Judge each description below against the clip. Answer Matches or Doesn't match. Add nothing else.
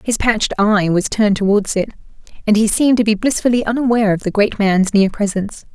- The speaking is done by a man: Doesn't match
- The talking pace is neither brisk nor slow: Doesn't match